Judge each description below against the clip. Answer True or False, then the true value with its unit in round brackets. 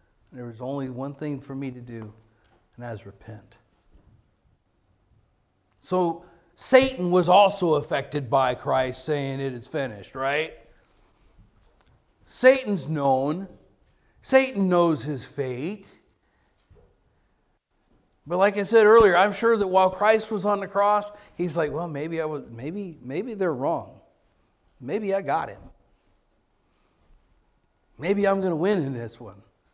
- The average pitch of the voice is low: False (155 Hz)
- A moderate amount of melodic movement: False (7.6 semitones)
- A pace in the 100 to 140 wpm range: True (135 wpm)